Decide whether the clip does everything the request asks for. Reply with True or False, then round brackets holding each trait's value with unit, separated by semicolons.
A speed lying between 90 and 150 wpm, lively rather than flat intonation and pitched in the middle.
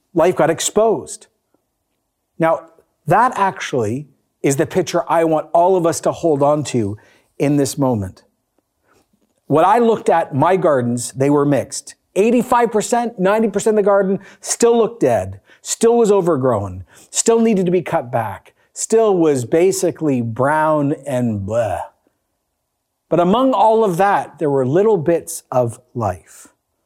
True (145 wpm; 7.4 semitones; 165 Hz)